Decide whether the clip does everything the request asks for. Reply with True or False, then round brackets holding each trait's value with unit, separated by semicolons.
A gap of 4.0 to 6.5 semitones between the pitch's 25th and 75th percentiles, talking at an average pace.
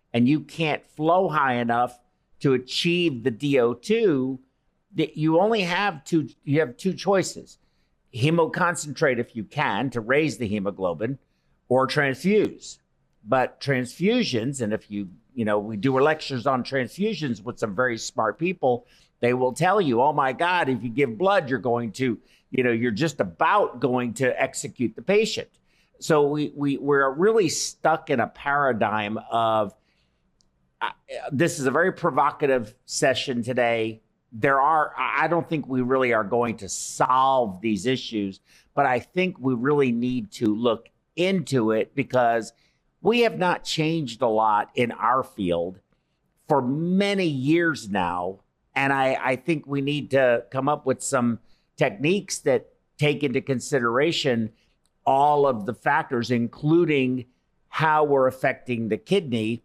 True (4.8 semitones; 150 wpm)